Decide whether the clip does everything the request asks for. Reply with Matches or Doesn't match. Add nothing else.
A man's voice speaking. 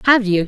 Doesn't match